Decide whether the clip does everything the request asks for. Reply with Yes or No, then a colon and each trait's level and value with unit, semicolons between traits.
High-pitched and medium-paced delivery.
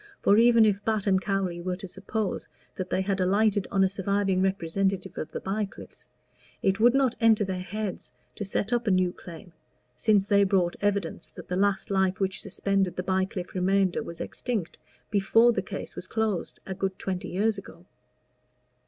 Yes: high, 195 Hz; average, 180 wpm